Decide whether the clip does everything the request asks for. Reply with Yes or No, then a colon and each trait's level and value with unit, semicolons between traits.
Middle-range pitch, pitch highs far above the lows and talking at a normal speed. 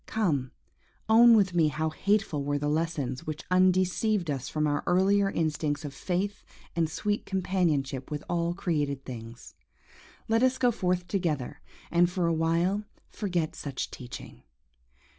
No: medium, 170 Hz; average, 4.5 semitones; average, 150 wpm